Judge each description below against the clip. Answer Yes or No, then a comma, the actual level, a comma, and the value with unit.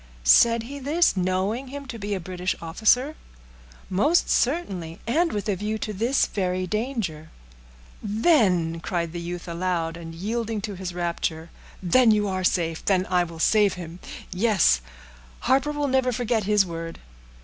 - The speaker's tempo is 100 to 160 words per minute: Yes, average, 155 wpm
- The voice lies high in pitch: Yes, high, 195 Hz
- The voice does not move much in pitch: No, average, 5.2 semitones